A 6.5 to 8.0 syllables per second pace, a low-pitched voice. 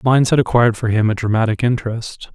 Yes: 6.8 syllables/s; low, 115 Hz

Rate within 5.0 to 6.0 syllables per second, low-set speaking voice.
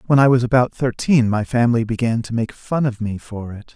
Yes: 5.6 syllables/s; low, 115 Hz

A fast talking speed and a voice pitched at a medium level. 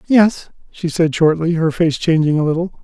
No: average, 190 wpm; medium, 165 Hz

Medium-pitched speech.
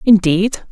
No: high, 200 Hz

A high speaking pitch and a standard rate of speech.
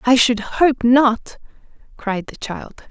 Yes: high, 240 Hz; average, 145 wpm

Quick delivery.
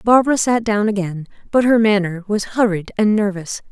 No: average, 180 wpm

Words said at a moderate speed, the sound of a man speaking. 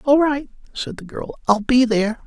No: fast, 210 wpm; male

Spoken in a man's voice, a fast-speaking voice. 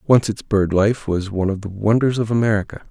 Yes: male; fast, 225 wpm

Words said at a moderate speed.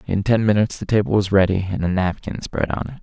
No: fast, 260 wpm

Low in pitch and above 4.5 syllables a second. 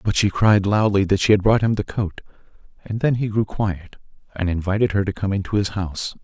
Yes: low, 100 Hz; 5.7 syllables/s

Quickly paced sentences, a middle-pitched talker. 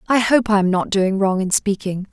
No: fast, 255 wpm; high, 200 Hz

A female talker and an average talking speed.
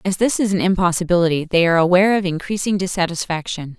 Yes: female; average, 175 wpm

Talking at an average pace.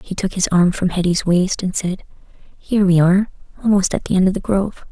No: fast, 230 wpm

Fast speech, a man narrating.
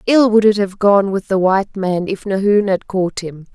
No: fast, 235 wpm; female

